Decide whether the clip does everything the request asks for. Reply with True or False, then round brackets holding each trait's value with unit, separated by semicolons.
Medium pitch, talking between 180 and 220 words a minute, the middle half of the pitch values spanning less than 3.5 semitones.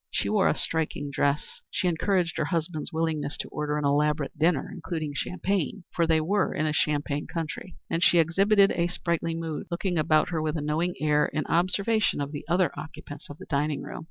True (160 Hz; 200 wpm; 2.7 semitones)